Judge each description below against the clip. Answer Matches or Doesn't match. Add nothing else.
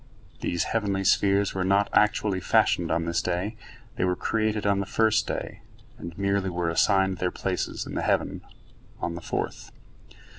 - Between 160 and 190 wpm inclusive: Matches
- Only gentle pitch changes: Matches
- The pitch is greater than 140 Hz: Doesn't match